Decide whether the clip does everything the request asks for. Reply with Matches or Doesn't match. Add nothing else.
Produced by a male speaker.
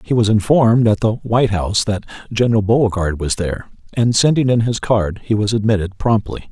Matches